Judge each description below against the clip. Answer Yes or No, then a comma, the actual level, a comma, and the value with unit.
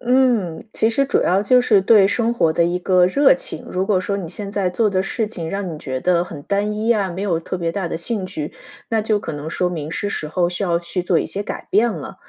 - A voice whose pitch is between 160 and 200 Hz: Yes, high, 190 Hz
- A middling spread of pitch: Yes, average, 3.8 semitones